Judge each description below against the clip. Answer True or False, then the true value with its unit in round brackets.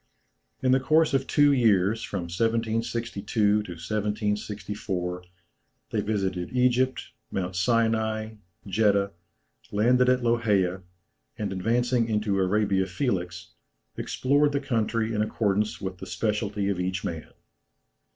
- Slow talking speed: True (115 wpm)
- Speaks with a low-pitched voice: True (105 Hz)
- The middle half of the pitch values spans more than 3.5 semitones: False (3.1 semitones)